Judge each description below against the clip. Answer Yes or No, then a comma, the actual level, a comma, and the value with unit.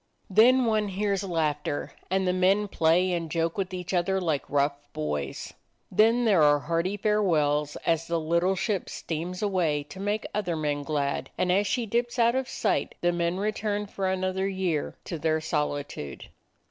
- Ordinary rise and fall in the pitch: Yes, average, 4.3 semitones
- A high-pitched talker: No, medium, 180 Hz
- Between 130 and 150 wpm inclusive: No, average, 175 wpm